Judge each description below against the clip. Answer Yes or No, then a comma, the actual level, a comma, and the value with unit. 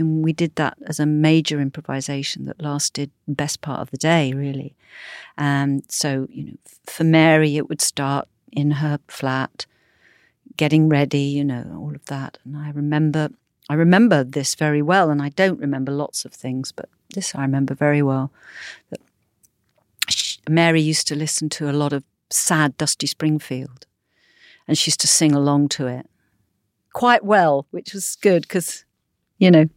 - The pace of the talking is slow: No, average, 175 wpm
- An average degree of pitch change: No, narrow, 2.0 semitones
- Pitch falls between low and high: Yes, medium, 145 Hz